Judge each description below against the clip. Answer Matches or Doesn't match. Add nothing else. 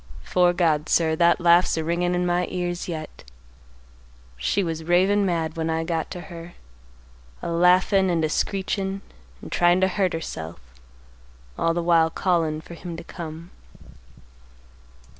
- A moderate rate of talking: Matches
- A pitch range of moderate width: Doesn't match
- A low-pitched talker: Doesn't match